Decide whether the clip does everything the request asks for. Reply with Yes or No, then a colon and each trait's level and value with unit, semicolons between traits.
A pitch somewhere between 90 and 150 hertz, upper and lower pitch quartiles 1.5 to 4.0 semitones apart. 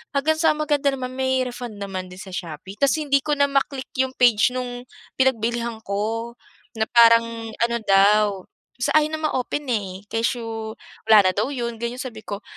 No: high, 235 Hz; average, 3.3 semitones